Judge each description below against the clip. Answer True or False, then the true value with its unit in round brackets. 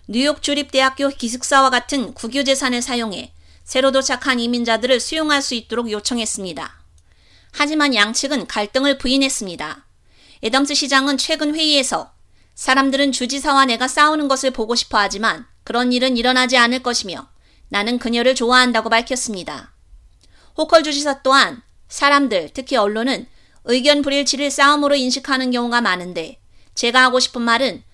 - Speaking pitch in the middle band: False (255 Hz)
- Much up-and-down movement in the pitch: False (3.1 semitones)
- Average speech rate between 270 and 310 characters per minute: False (350 characters per minute)